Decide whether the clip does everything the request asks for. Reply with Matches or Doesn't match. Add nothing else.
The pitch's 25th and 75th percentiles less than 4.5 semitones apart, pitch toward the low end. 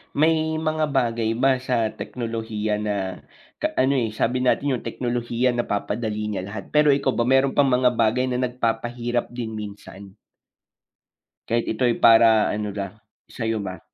Matches